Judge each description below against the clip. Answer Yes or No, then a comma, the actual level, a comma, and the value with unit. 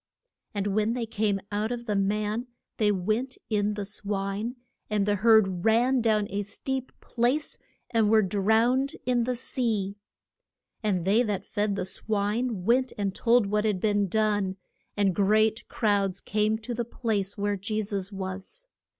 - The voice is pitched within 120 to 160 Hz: No, high, 210 Hz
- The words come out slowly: No, average, 160 wpm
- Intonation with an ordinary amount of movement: No, narrow, 2.3 semitones